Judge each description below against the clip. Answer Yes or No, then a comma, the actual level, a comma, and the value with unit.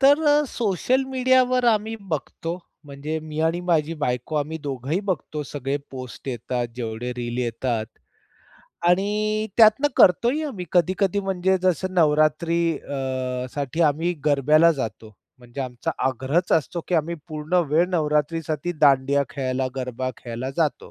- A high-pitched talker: No, medium, 155 Hz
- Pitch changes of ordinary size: No, wide, 5.7 semitones